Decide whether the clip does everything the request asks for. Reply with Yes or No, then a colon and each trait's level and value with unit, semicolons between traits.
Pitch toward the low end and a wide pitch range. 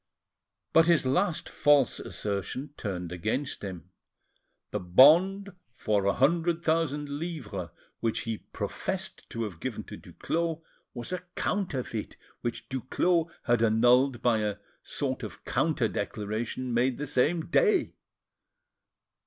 Yes: low, 130 Hz; wide, 7.0 semitones